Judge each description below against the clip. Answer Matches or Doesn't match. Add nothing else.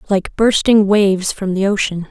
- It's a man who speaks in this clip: Doesn't match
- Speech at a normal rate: Matches